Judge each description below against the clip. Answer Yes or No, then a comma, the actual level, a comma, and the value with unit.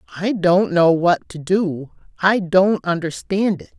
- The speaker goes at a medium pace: Yes, average, 160 wpm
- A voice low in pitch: No, medium, 180 Hz